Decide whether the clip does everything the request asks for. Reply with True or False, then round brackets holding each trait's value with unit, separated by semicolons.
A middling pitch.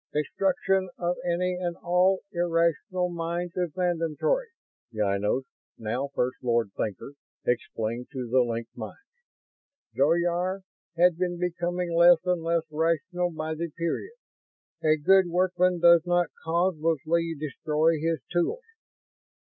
True (170 Hz)